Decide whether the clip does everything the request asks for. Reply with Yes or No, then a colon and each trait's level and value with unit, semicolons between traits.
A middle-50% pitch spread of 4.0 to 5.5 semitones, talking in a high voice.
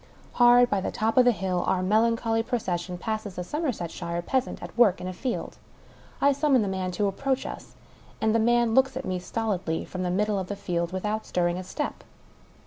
Yes: average, 4.7 semitones; high, 210 Hz